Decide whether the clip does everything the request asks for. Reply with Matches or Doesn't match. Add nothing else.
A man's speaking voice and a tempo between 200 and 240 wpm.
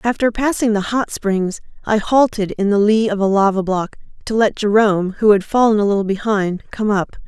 Doesn't match